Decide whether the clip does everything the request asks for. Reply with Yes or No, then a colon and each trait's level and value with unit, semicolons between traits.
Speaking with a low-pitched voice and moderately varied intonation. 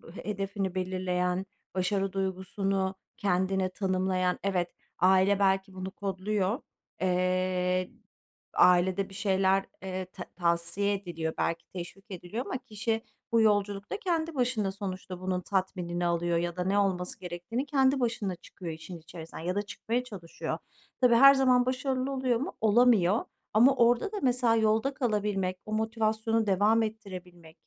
No: high, 195 Hz; average, 3.4 semitones